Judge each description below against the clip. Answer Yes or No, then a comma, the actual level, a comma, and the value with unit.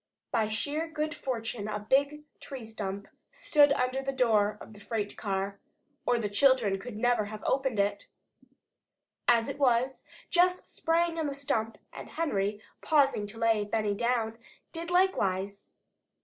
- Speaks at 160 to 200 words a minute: No, average, 150 wpm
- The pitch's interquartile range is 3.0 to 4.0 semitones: No, average, 5.2 semitones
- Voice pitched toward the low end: No, high, 235 Hz